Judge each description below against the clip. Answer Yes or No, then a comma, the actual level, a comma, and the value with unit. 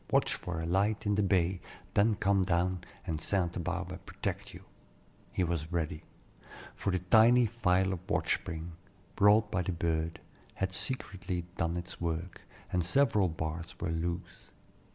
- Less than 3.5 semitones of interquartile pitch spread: Yes, average, 2.9 semitones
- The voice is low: Yes, very low, 90 Hz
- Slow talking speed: No, average, 155 wpm